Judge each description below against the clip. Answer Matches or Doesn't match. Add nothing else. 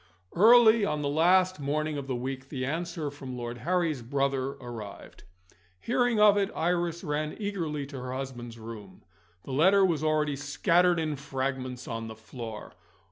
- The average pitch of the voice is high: Doesn't match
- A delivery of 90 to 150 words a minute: Doesn't match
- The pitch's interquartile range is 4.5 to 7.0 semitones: Matches